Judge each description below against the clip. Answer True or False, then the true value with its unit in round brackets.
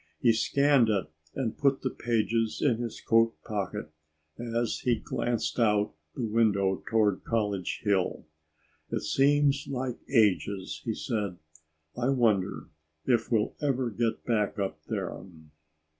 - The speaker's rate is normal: False (130 wpm)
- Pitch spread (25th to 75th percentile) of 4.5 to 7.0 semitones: False (3.0 semitones)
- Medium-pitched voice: False (115 Hz)